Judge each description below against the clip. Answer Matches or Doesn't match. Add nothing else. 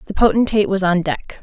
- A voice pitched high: Matches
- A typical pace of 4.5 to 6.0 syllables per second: Doesn't match